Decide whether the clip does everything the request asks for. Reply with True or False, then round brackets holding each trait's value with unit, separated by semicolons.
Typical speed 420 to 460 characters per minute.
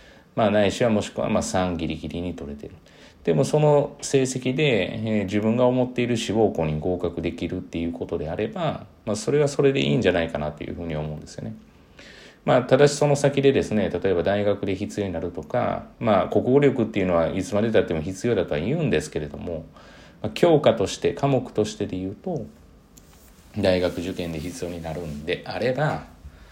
False (395 characters per minute)